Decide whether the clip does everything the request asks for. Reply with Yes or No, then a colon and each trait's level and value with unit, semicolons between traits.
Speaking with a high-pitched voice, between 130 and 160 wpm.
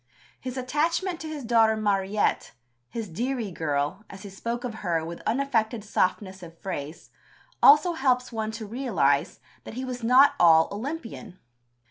Yes: high, 225 Hz; average, 150 wpm